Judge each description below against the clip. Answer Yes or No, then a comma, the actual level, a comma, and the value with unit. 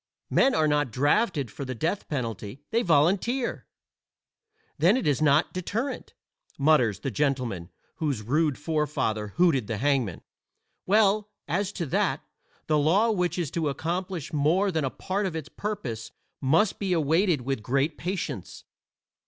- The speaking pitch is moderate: Yes, medium, 155 Hz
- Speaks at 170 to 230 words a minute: No, average, 145 wpm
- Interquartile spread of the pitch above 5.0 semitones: Yes, wide, 5.4 semitones